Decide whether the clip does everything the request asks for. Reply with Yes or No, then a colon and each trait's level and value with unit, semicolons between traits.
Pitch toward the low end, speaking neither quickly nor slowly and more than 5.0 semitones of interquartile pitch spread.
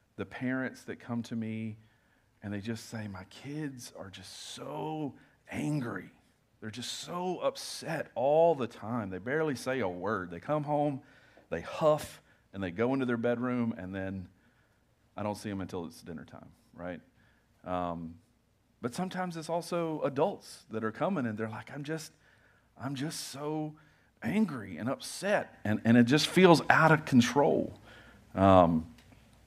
Yes: low, 120 Hz; average, 160 wpm; wide, 5.5 semitones